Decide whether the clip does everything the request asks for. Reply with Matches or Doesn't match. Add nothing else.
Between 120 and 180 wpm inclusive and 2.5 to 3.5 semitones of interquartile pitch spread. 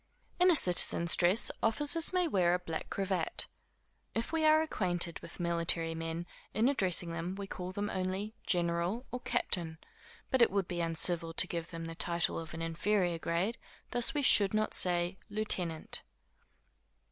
Doesn't match